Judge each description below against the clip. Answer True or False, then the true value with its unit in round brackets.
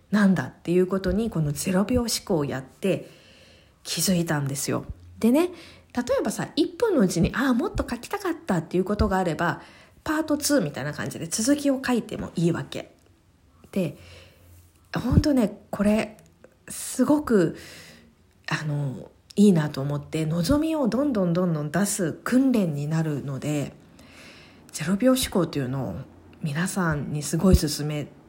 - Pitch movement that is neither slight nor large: False (7.8 semitones)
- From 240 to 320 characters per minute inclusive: True (295 characters per minute)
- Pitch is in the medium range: True (175 Hz)